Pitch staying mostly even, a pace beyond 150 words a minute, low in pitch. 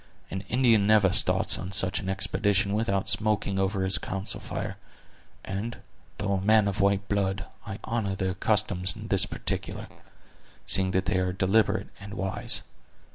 Yes: narrow, 1.5 semitones; average, 160 wpm; low, 100 Hz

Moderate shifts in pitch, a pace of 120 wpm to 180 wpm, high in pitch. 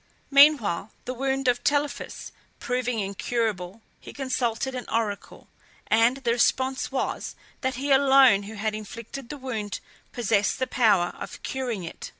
Yes: average, 3.6 semitones; average, 145 wpm; high, 245 Hz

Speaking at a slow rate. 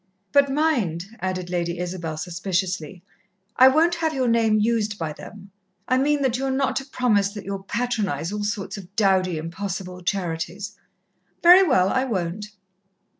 No: average, 160 wpm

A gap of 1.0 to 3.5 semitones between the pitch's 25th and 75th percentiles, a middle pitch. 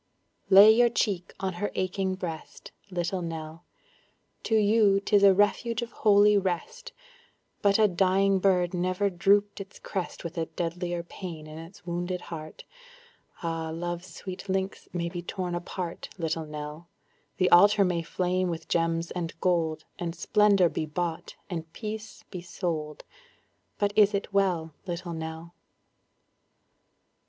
Yes: average, 2.9 semitones; medium, 180 Hz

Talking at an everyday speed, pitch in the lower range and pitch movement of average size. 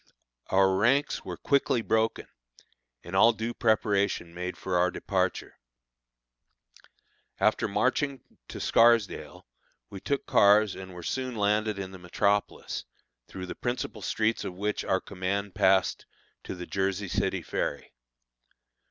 No: slow, 130 wpm; low, 100 Hz; average, 3.0 semitones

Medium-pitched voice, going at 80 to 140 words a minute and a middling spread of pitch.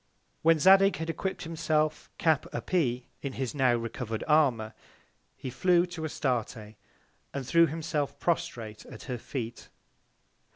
Yes: medium, 145 Hz; slow, 135 wpm; average, 5.0 semitones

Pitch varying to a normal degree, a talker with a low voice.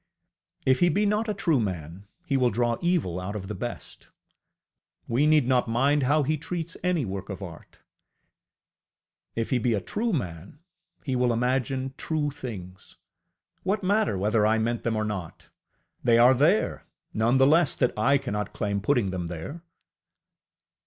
No: wide, 6.1 semitones; low, 125 Hz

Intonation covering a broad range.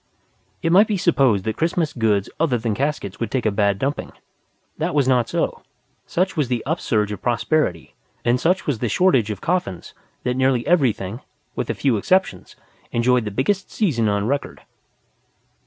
Yes: wide, 6.5 semitones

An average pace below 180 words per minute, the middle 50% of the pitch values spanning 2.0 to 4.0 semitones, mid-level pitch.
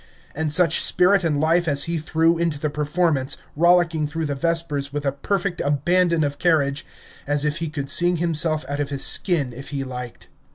No: average, 195 wpm; average, 2.9 semitones; medium, 155 Hz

